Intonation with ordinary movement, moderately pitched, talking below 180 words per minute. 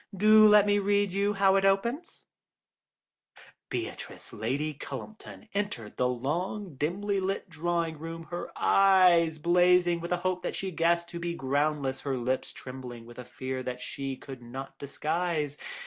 No: wide, 6.2 semitones; medium, 170 Hz; average, 155 wpm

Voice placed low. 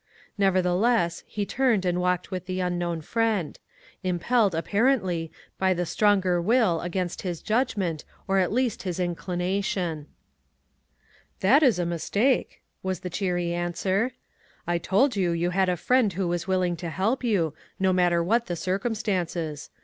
No: medium, 185 Hz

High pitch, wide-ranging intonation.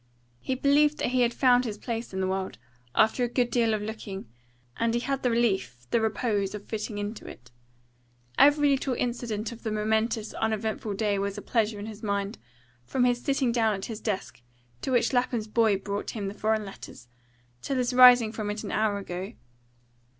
No: high, 220 Hz; average, 3.0 semitones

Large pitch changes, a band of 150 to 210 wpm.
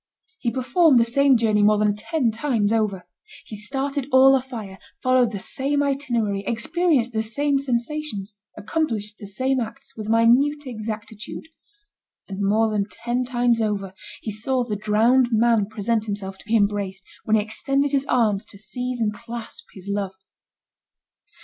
No: average, 3.8 semitones; average, 155 wpm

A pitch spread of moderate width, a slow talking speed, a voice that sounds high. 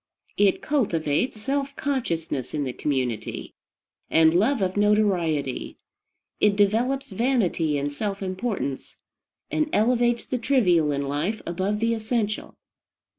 No: wide, 6.8 semitones; slow, 120 wpm; high, 200 Hz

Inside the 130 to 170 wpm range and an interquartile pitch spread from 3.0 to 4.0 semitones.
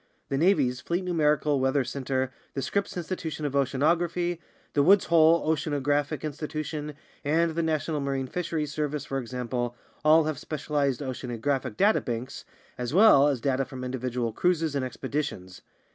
Yes: average, 145 wpm; average, 3.5 semitones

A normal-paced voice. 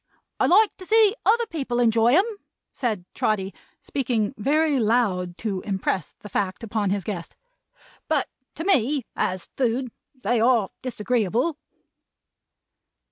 No: slow, 130 wpm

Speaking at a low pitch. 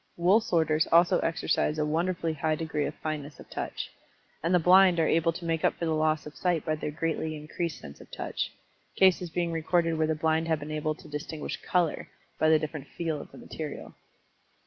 No: medium, 160 Hz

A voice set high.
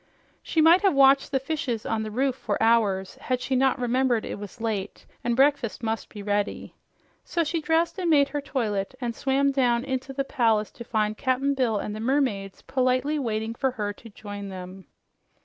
Yes: high, 245 Hz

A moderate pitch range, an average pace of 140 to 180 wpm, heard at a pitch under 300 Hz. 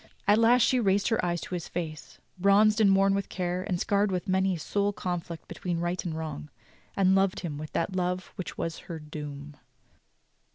No: average, 3.0 semitones; average, 200 wpm; medium, 185 Hz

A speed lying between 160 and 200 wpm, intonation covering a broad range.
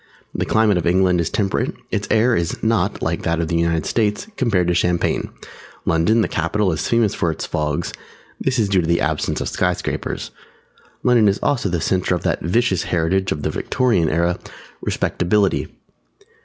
No: average, 180 wpm; average, 4.3 semitones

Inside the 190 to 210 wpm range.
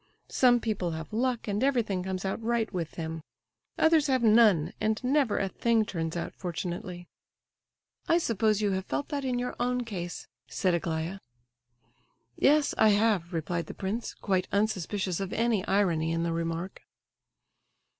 No: average, 155 wpm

